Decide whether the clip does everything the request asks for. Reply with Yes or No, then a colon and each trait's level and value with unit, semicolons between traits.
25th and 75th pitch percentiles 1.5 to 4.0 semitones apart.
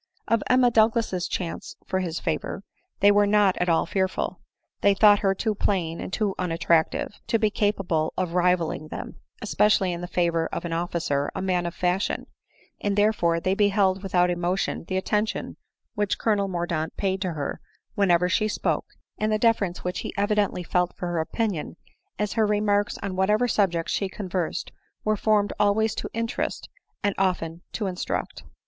Yes: average, 3.0 semitones